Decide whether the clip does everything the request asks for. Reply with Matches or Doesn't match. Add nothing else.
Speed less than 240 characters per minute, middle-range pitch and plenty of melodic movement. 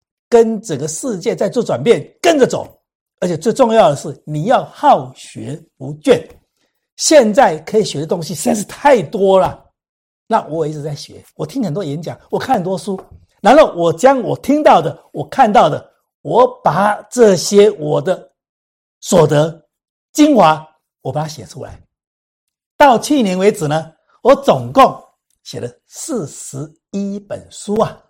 Matches